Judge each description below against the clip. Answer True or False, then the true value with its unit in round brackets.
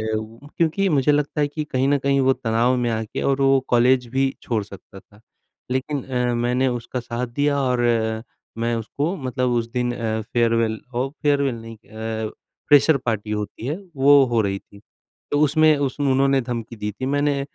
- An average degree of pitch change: True (3.4 semitones)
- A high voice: False (125 Hz)